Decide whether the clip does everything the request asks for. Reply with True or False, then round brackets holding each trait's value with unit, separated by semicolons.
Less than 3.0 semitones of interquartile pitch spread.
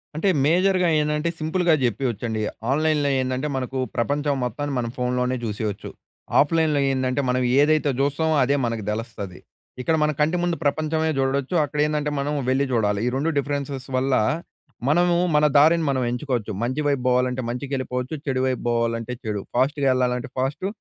False (3.3 semitones)